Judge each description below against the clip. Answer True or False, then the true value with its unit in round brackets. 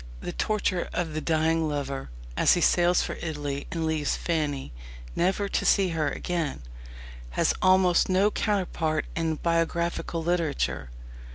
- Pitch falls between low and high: True (165 Hz)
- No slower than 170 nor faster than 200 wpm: False (140 wpm)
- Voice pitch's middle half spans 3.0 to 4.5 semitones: False (2.6 semitones)